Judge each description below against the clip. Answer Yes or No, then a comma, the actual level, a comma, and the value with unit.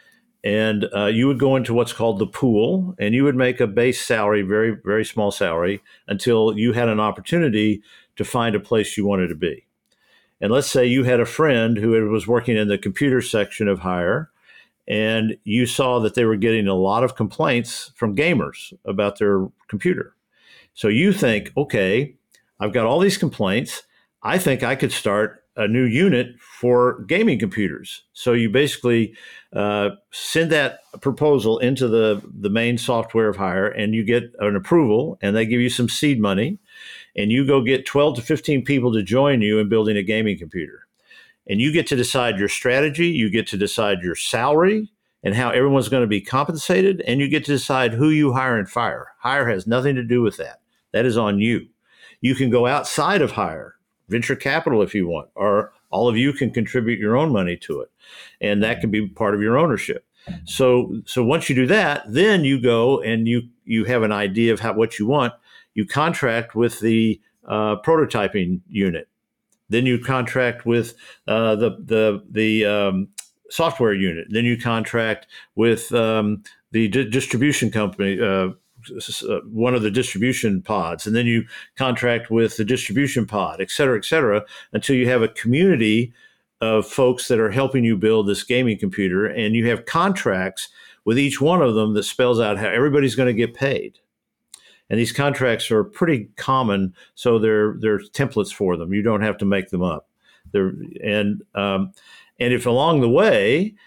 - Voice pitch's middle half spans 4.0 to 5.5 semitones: No, average, 3.4 semitones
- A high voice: No, low, 115 Hz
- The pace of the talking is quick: No, average, 185 wpm